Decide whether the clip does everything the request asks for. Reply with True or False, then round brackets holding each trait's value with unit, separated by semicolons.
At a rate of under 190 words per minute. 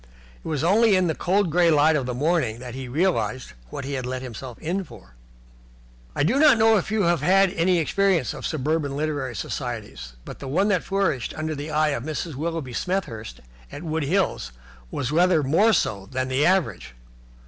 False (195 wpm)